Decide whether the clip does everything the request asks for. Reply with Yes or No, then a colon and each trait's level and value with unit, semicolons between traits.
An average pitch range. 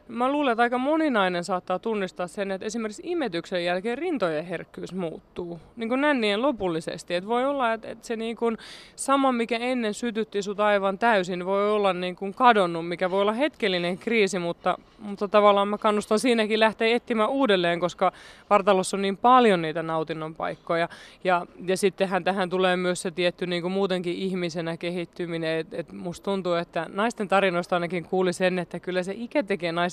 Yes: average, 4.2 semitones